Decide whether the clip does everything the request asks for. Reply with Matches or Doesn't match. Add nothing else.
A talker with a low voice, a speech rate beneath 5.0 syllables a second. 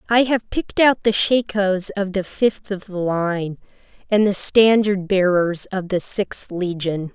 Doesn't match